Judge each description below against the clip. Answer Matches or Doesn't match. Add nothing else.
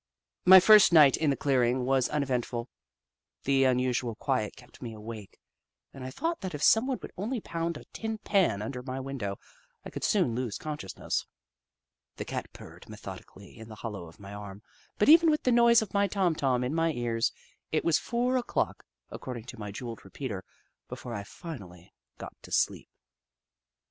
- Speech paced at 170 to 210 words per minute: Matches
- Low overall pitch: Matches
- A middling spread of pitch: Doesn't match